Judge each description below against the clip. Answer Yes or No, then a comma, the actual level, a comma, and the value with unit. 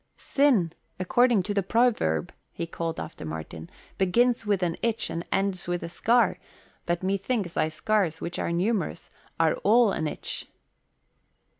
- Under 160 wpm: Yes, average, 150 wpm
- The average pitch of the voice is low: No, medium, 185 Hz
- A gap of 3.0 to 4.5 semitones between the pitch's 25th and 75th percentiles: No, average, 5.1 semitones